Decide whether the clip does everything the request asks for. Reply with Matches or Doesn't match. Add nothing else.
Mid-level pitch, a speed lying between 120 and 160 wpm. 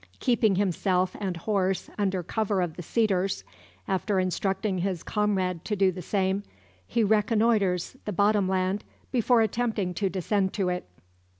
Doesn't match